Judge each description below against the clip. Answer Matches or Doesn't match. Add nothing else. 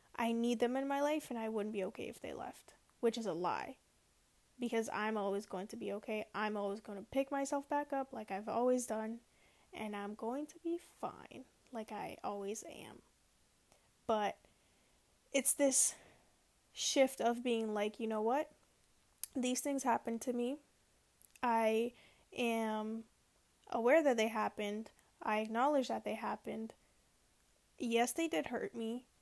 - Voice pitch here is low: Doesn't match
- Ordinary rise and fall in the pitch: Matches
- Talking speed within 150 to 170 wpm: Matches